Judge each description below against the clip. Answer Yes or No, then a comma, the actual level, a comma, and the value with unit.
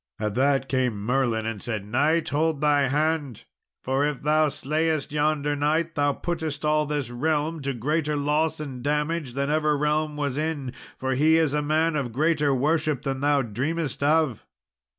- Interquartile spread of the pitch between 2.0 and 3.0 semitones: Yes, narrow, 2.4 semitones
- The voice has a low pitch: No, medium, 145 Hz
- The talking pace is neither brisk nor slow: Yes, average, 170 wpm